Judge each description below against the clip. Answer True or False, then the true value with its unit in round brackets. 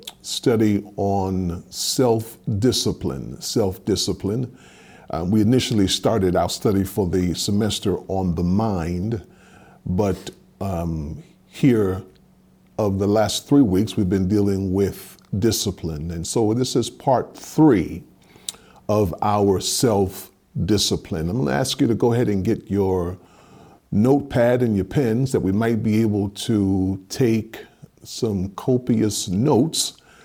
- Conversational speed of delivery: False (125 wpm)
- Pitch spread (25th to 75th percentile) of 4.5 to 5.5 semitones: False (3.1 semitones)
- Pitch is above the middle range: False (100 Hz)